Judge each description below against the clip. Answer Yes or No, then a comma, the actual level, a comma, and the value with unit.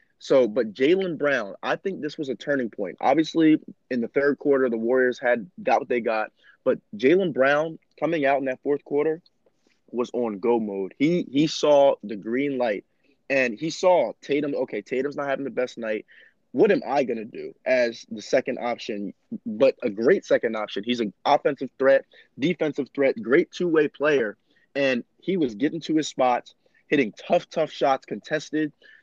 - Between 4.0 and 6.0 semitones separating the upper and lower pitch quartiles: Yes, average, 4.6 semitones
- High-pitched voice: No, medium, 140 Hz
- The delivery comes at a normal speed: Yes, average, 180 wpm